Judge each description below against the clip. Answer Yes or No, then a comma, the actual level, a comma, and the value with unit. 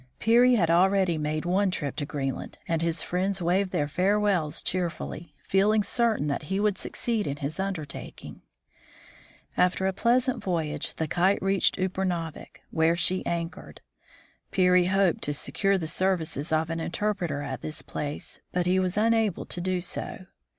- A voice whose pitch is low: No, medium, 180 Hz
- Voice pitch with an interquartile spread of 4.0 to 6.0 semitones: No, average, 3.4 semitones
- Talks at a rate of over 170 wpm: No, average, 165 wpm